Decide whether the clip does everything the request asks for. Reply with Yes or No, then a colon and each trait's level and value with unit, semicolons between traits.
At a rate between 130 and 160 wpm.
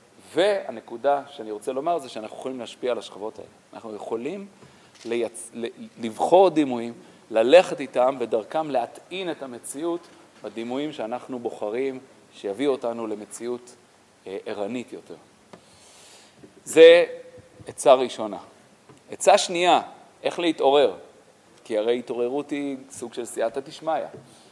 No: average, 110 wpm